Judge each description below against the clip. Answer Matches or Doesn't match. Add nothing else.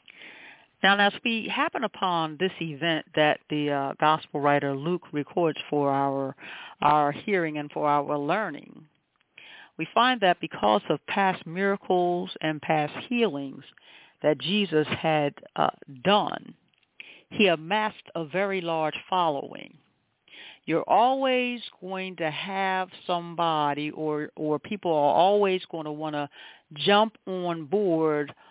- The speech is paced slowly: Matches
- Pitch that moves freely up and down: Doesn't match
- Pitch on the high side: Doesn't match